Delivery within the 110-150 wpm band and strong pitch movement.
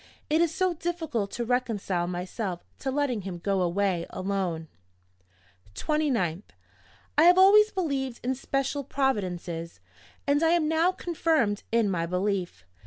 Yes: slow, 135 wpm; wide, 9.0 semitones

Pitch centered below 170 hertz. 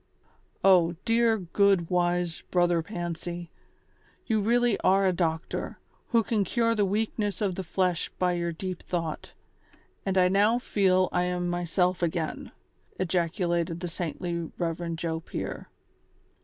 No: medium, 180 Hz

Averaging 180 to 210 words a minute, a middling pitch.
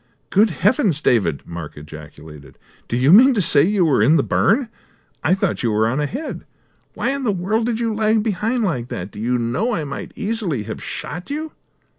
Yes: average, 200 wpm; medium, 175 Hz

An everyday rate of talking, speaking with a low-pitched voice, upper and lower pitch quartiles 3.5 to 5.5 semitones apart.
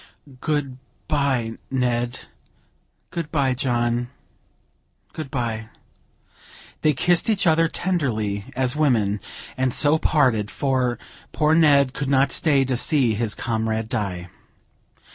No: slow, 115 wpm; low, 130 Hz; average, 4.2 semitones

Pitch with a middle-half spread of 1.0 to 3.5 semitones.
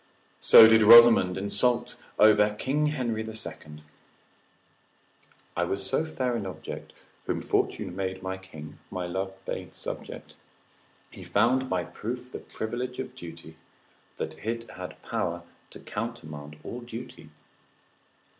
No: average, 4.5 semitones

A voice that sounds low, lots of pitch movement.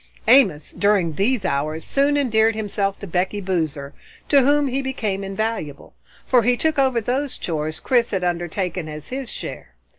No: high, 205 Hz; wide, 6.9 semitones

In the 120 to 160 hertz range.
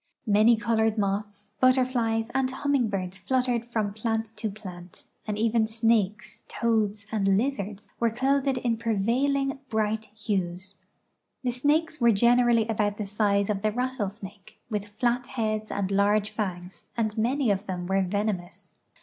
No: high, 220 Hz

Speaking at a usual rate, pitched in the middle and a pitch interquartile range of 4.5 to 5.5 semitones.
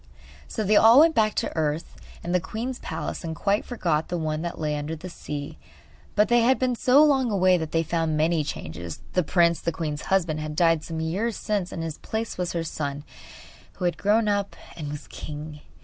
No: fast, 215 wpm; medium, 170 Hz; average, 5.2 semitones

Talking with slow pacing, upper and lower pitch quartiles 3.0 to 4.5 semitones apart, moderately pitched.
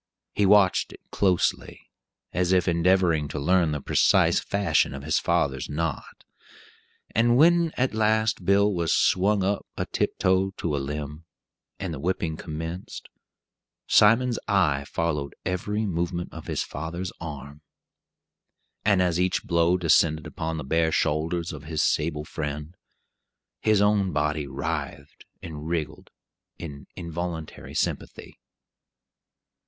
No: slow, 130 wpm; average, 3.7 semitones; very low, 85 Hz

